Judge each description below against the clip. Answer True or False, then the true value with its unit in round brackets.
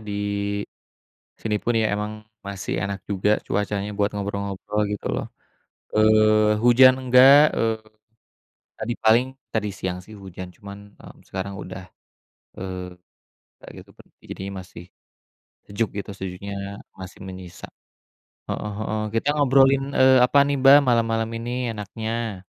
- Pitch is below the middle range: True (105 Hz)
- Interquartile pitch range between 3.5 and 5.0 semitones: False (2.9 semitones)